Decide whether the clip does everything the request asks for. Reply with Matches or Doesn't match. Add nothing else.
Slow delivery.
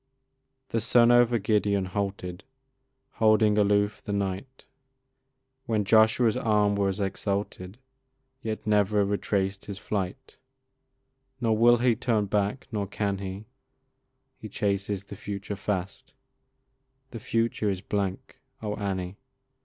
Matches